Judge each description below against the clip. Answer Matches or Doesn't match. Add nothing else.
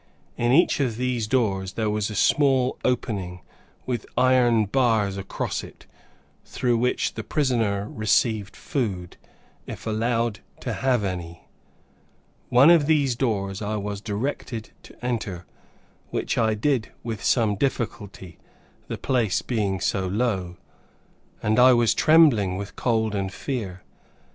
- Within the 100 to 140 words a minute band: Matches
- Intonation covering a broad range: Doesn't match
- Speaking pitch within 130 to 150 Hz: Doesn't match